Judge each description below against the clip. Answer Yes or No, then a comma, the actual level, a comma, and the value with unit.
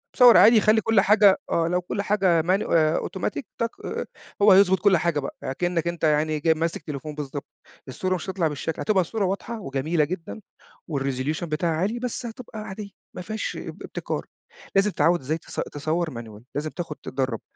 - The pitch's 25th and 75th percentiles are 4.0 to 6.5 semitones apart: Yes, average, 4.6 semitones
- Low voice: No, medium, 170 Hz